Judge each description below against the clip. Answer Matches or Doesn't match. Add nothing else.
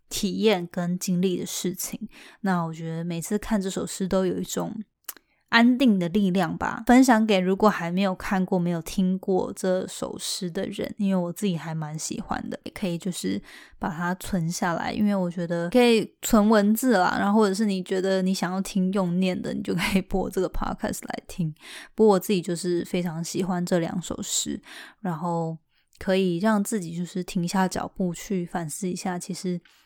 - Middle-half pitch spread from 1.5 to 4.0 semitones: Matches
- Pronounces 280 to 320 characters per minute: Matches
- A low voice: Doesn't match